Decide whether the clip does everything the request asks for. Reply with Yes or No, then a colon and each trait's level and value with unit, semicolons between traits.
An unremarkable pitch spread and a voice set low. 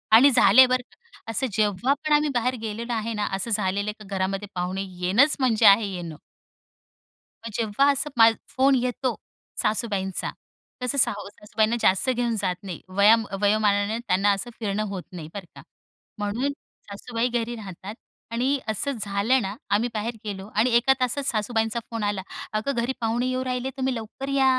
No: average, 3.8 semitones; high, 225 Hz